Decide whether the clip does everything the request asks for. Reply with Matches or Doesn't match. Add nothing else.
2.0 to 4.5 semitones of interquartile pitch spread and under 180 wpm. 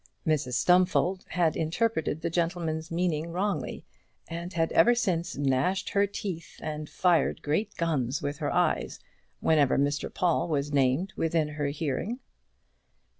Matches